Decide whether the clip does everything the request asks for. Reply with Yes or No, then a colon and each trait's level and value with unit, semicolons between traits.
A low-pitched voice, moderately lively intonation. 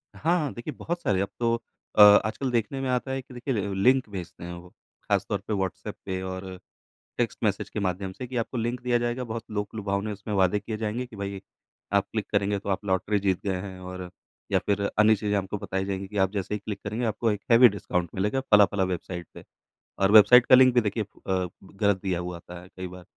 Yes: low, 100 Hz; average, 3.5 semitones